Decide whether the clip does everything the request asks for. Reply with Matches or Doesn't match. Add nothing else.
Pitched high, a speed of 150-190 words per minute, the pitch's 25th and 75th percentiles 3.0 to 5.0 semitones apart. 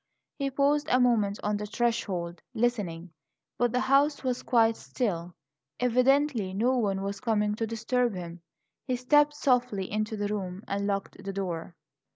Matches